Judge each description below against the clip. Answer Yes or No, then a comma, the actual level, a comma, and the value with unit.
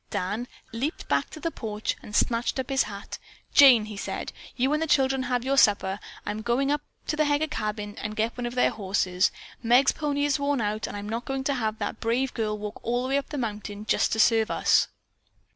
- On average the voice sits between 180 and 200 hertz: No, high, 235 Hz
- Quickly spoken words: Yes, fast, 230 wpm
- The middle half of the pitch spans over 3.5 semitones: Yes, average, 4.3 semitones